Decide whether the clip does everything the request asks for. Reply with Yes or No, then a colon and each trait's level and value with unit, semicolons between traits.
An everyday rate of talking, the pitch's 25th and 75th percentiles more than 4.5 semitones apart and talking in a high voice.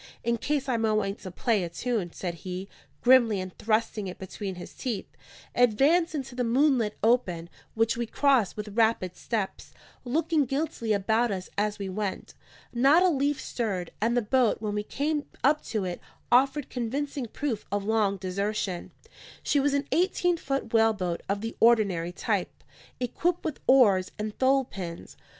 Yes: average, 170 wpm; average, 5.2 semitones; high, 225 Hz